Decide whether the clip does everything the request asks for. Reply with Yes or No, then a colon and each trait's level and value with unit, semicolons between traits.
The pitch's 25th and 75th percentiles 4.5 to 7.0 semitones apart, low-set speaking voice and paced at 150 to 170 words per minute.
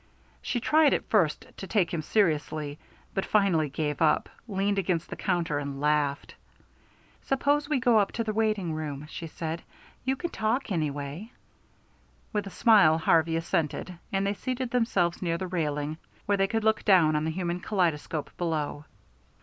No: wide, 5.4 semitones; medium, 175 Hz; average, 165 wpm